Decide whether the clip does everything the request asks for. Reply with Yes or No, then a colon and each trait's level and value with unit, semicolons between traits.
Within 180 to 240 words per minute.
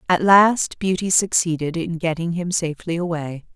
No: average, 150 wpm